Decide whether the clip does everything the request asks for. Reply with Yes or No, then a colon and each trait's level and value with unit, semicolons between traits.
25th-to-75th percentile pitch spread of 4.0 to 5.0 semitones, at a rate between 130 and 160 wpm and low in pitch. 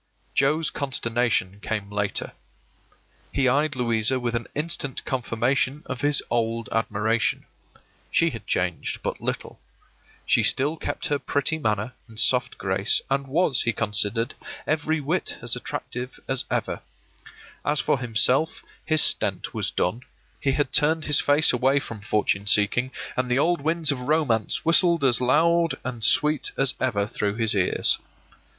Yes: average, 4.5 semitones; average, 150 wpm; low, 130 Hz